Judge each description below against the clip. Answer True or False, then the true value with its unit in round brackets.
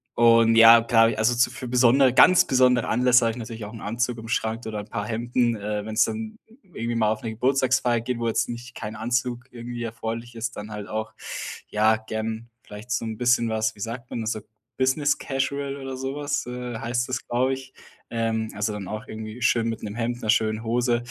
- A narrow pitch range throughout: True (2.0 semitones)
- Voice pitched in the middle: False (115 Hz)